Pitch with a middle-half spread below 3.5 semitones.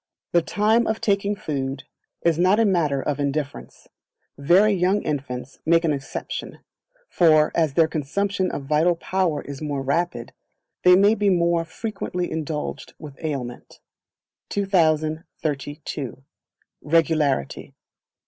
No: average, 4.3 semitones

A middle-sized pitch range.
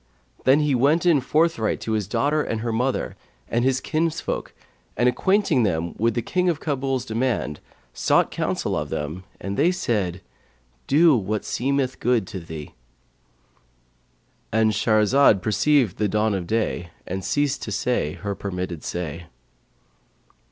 No: wide, 6.7 semitones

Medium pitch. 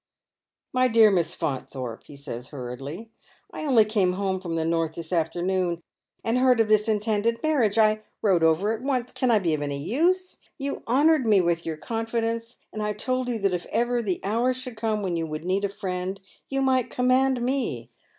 No: high, 210 Hz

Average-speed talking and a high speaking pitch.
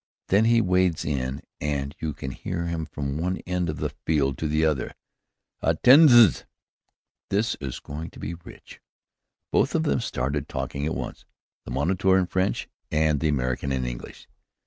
No: average, 170 wpm; very low, 80 Hz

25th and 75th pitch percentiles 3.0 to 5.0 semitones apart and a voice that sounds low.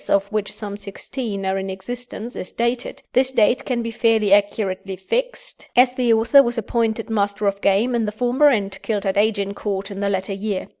No: average, 3.3 semitones; high, 215 Hz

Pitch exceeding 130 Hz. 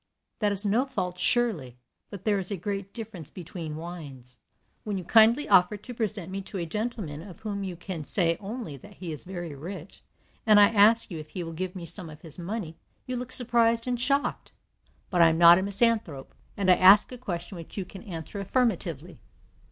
Yes: high, 190 Hz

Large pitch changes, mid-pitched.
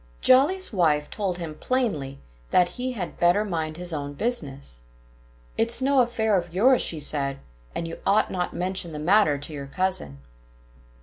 Yes: wide, 6.7 semitones; medium, 175 Hz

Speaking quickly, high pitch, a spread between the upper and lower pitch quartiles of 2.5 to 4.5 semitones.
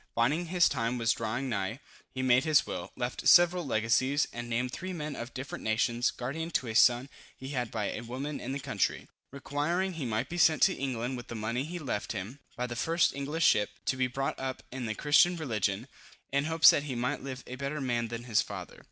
No: fast, 220 wpm; low, 130 Hz; average, 3.7 semitones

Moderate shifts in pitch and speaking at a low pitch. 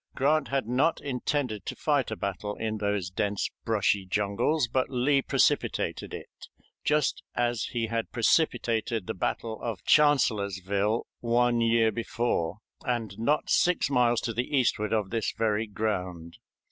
Yes: average, 3.2 semitones; low, 115 Hz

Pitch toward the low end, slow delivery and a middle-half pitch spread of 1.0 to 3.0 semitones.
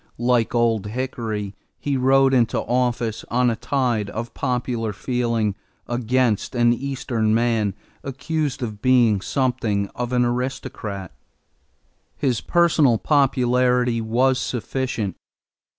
Yes: low, 120 Hz; slow, 110 wpm; narrow, 2.5 semitones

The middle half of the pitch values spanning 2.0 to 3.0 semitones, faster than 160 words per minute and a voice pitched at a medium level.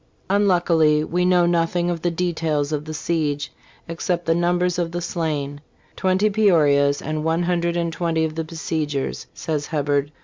Yes: narrow, 2.4 semitones; average, 170 wpm; medium, 165 Hz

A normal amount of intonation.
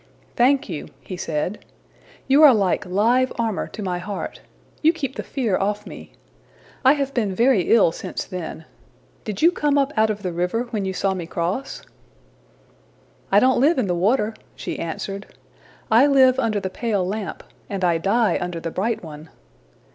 No: wide, 5.8 semitones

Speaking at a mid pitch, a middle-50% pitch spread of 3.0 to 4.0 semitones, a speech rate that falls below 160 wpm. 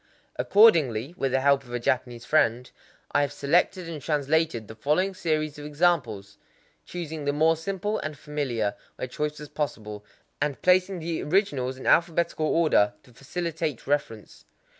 No: medium, 150 Hz; average, 4.5 semitones; average, 150 wpm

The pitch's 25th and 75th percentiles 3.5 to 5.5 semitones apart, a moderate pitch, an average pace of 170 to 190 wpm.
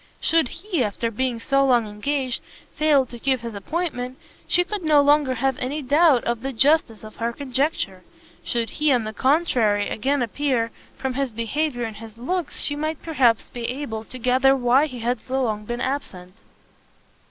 No: average, 3.9 semitones; very high, 255 Hz; average, 180 wpm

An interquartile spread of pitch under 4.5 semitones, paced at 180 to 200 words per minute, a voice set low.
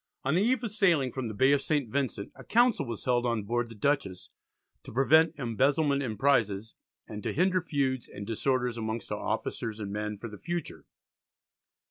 No: average, 4.8 semitones; average, 190 wpm; low, 130 Hz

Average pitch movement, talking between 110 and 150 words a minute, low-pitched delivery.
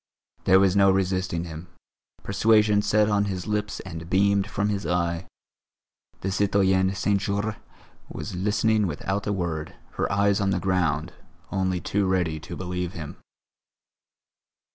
No: narrow, 2.2 semitones; average, 140 wpm; very low, 95 Hz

